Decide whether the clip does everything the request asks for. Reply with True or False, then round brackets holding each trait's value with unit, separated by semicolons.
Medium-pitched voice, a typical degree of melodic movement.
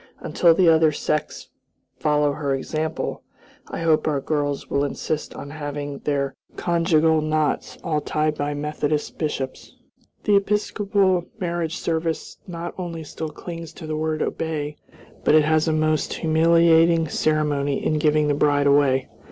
False (155 Hz; 2.0 semitones)